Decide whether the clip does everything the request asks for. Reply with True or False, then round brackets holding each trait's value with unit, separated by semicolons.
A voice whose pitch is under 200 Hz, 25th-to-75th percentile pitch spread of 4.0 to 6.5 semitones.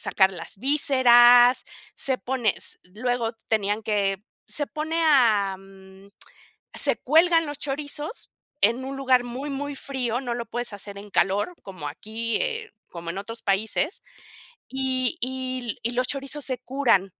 False (245 Hz; 4.9 semitones)